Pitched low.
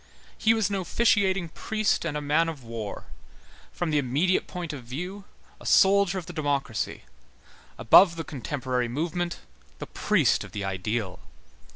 No: medium, 160 Hz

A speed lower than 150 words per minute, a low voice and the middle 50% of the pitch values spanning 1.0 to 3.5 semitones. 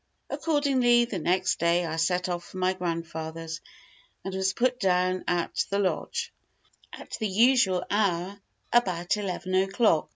No: average, 140 wpm; medium, 185 Hz; average, 3.2 semitones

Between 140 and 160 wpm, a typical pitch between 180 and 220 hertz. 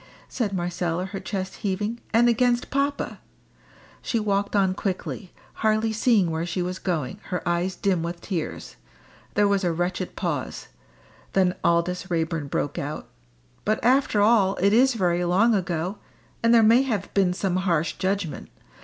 Yes: average, 155 wpm; high, 190 Hz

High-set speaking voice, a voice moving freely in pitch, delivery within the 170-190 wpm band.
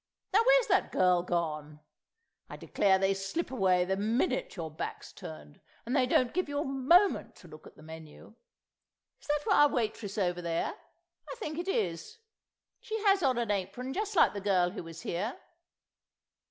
Yes: high, 205 Hz; wide, 8.5 semitones; average, 180 wpm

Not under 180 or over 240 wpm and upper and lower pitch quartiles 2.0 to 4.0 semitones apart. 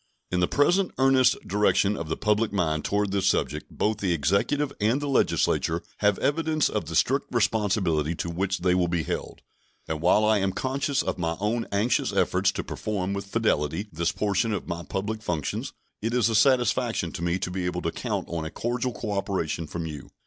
No: average, 200 wpm; average, 5.0 semitones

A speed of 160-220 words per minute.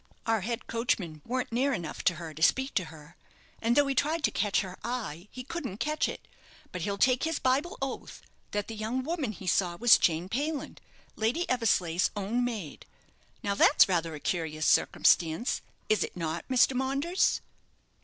Yes: average, 180 wpm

